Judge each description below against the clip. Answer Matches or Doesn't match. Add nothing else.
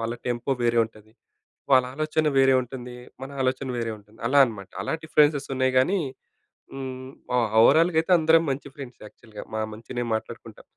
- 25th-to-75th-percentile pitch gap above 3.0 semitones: Matches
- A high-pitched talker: Doesn't match